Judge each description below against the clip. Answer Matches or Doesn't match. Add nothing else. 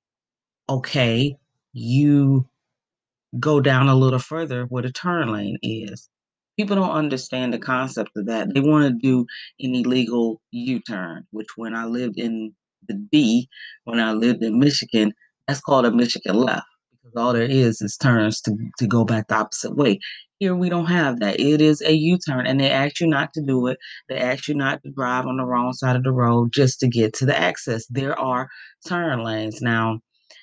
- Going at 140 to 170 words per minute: Doesn't match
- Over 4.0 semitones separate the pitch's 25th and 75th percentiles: Doesn't match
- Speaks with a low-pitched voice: Matches